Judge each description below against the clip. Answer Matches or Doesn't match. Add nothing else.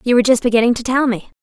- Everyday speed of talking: Doesn't match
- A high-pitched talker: Matches